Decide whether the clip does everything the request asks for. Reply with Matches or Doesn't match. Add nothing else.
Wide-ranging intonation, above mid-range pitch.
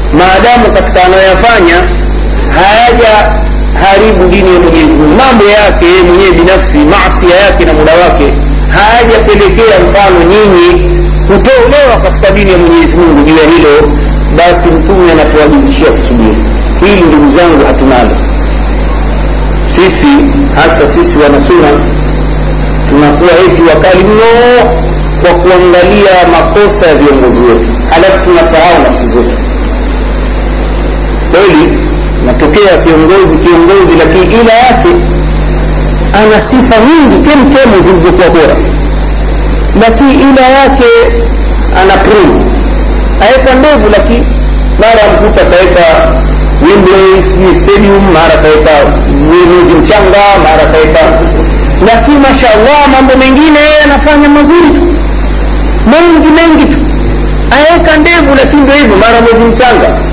Matches